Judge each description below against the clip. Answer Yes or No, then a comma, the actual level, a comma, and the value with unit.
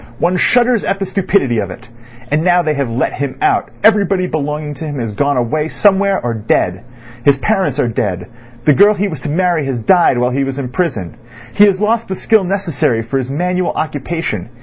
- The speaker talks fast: Yes, fast, 210 wpm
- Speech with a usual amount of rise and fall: No, wide, 6.9 semitones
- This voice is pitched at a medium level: Yes, medium, 155 Hz